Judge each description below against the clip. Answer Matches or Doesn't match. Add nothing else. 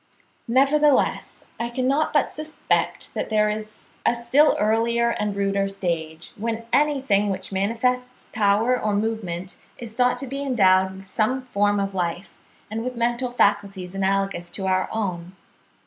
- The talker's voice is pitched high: Matches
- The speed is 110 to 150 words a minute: Matches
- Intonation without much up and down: Doesn't match